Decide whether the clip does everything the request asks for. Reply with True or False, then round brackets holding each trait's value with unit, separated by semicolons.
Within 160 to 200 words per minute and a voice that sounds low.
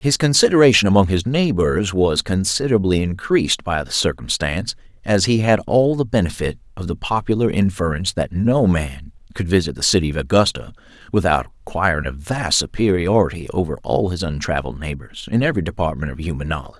True (165 wpm; 95 Hz)